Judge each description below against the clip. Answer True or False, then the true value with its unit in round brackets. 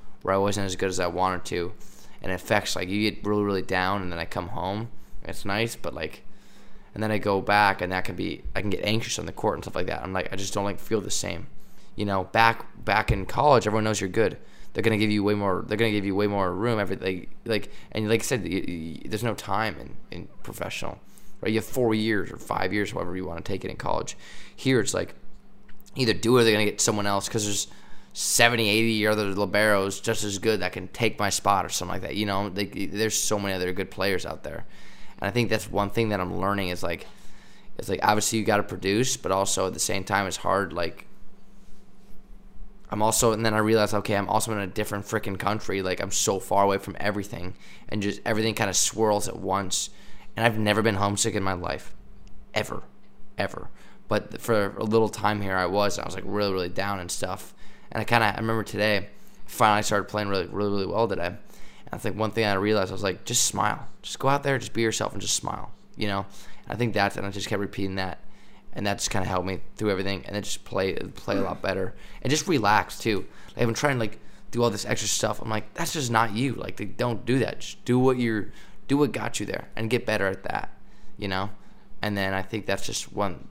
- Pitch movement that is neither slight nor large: False (2.3 semitones)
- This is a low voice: True (105 Hz)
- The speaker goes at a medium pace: False (250 wpm)